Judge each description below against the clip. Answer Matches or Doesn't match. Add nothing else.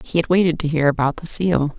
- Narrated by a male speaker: Doesn't match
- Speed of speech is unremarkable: Doesn't match